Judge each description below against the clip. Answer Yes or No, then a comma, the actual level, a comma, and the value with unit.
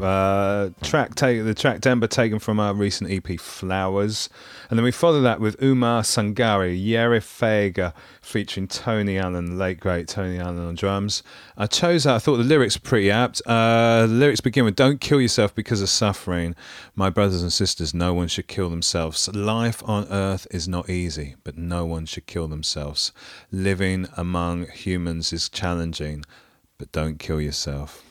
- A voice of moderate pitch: No, very low, 95 Hz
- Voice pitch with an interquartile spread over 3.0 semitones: Yes, average, 4.5 semitones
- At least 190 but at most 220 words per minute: No, average, 175 wpm